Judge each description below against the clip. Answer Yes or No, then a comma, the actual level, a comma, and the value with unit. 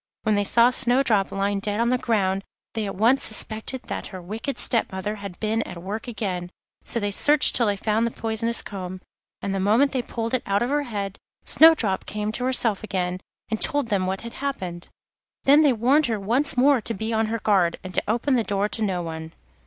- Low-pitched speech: No, high, 220 Hz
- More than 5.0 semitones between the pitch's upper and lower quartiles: No, average, 3.5 semitones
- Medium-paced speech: No, fast, 220 wpm